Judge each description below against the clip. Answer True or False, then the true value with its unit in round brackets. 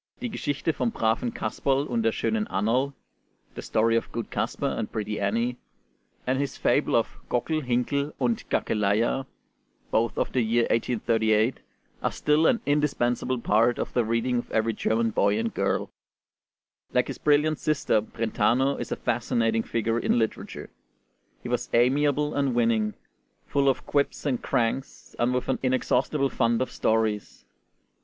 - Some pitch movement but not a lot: True (3.6 semitones)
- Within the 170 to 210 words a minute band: False (155 wpm)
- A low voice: True (120 Hz)